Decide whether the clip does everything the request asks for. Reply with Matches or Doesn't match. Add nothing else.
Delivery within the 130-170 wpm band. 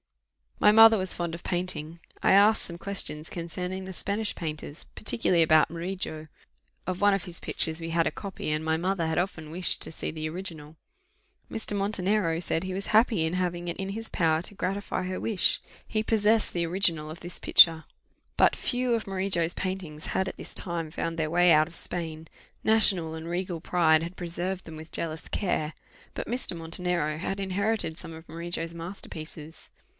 Doesn't match